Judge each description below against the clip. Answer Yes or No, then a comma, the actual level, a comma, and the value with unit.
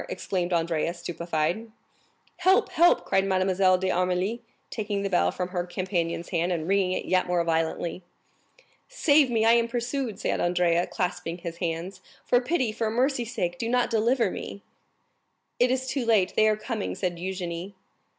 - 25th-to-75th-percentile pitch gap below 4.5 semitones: No, average, 4.9 semitones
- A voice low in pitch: No, high, 190 Hz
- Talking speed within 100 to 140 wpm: No, average, 165 wpm